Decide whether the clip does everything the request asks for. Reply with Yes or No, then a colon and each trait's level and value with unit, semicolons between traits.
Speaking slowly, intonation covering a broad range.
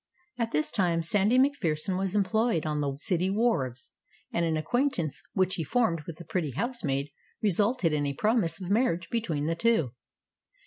No: average, 170 wpm; wide, 6.2 semitones